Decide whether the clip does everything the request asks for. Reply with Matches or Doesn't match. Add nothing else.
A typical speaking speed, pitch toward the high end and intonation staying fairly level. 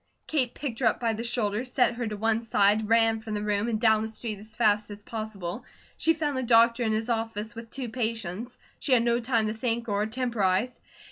Doesn't match